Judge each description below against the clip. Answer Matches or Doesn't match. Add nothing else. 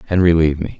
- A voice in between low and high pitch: Doesn't match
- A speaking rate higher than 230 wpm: Doesn't match